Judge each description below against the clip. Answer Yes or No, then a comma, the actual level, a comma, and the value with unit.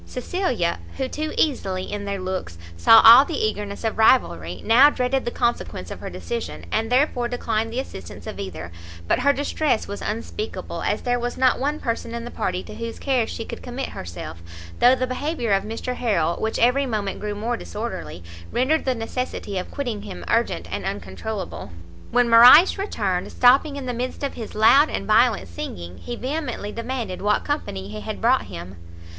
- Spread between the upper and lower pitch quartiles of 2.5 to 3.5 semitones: No, average, 4.4 semitones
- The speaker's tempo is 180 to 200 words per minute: Yes, average, 185 wpm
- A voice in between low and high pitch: No, high, 230 Hz